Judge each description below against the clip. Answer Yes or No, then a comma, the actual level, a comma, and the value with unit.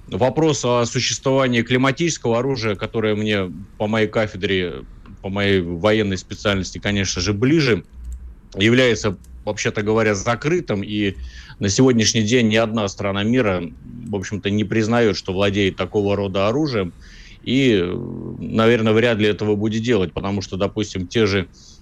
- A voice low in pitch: Yes, low, 105 Hz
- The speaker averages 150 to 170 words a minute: No, average, 140 wpm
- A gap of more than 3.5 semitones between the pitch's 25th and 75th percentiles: No, average, 2.9 semitones